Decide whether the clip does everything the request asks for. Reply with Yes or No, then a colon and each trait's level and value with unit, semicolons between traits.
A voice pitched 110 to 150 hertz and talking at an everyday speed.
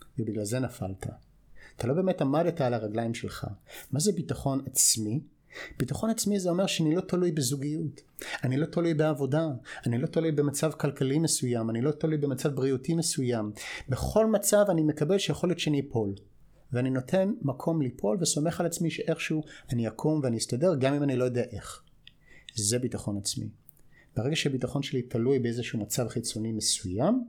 No: medium, 140 Hz; fast, 165 wpm